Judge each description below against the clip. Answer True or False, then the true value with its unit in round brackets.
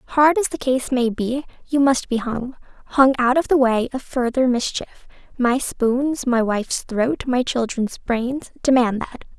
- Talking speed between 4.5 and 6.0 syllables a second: False (4.2 syllables/s)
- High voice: True (255 Hz)